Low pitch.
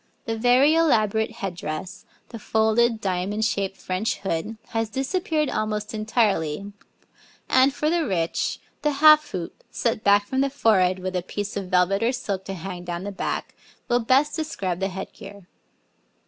No: high, 210 Hz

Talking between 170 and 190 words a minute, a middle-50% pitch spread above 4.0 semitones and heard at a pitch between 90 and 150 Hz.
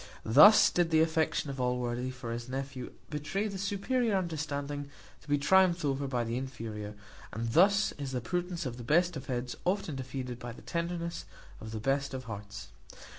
Yes: average, 180 wpm; wide, 5.6 semitones; medium, 140 Hz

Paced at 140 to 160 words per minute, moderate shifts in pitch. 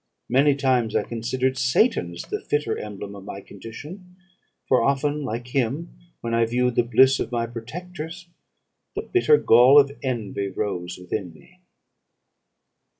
Yes: average, 150 wpm; average, 4.5 semitones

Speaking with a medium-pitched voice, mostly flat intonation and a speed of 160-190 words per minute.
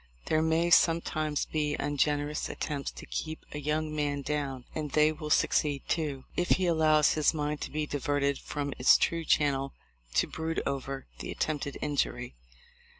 Yes: medium, 150 Hz; narrow, 1.6 semitones; average, 165 wpm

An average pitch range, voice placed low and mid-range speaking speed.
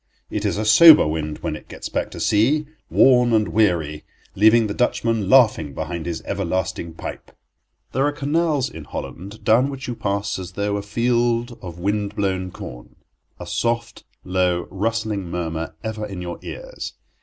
Yes: average, 4.8 semitones; low, 105 Hz; average, 165 wpm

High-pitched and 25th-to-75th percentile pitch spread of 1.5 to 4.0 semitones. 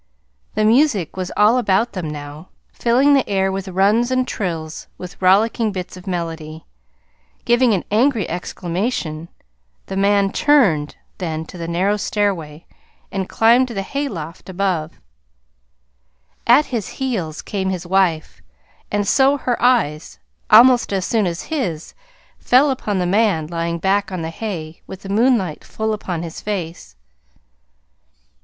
No: high, 195 Hz; average, 5.2 semitones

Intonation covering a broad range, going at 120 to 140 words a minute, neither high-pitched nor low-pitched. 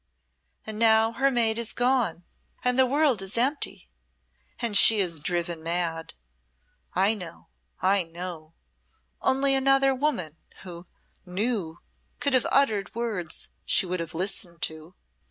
No: wide, 6.2 semitones; slow, 135 wpm; high, 200 Hz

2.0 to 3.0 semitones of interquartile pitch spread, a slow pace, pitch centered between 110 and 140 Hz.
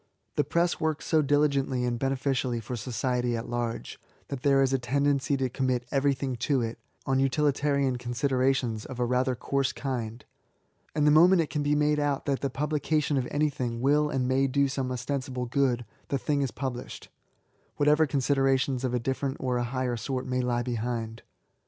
No: narrow, 2.5 semitones; average, 185 wpm; low, 135 Hz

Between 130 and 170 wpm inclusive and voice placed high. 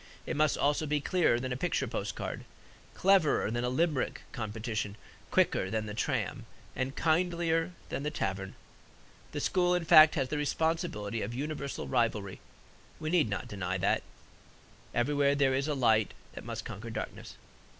No: average, 160 wpm; low, 135 Hz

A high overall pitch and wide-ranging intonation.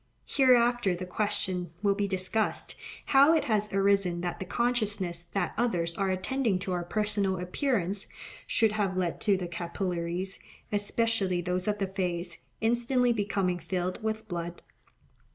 No: high, 195 Hz; average, 3.3 semitones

